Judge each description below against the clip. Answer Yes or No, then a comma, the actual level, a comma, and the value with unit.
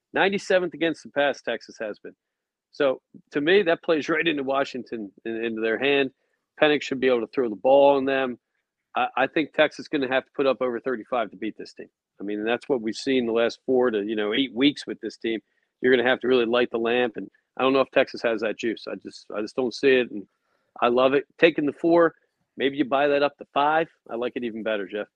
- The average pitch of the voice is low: Yes, low, 130 Hz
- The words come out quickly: Yes, fast, 260 wpm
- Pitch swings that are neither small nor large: Yes, average, 3.5 semitones